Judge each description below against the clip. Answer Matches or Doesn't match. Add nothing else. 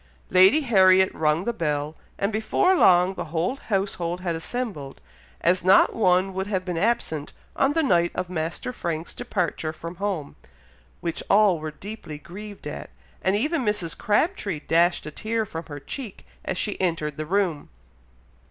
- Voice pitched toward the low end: Doesn't match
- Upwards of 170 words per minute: Doesn't match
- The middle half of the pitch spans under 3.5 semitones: Doesn't match